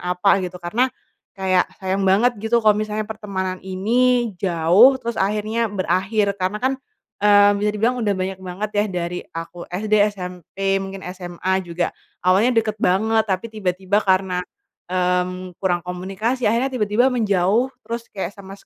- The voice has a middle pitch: No, high, 195 Hz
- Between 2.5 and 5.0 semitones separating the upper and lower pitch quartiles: Yes, average, 2.9 semitones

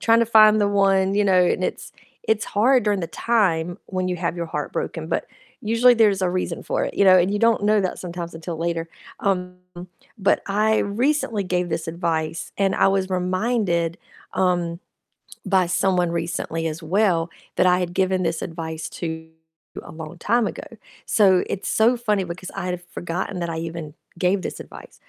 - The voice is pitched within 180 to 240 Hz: Yes, medium, 185 Hz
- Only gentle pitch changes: No, average, 3.2 semitones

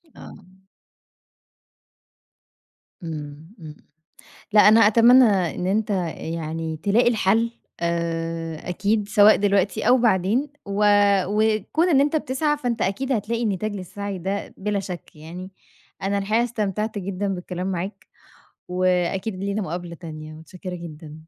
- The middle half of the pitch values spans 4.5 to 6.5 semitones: No, average, 4.0 semitones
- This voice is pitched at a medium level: No, high, 195 Hz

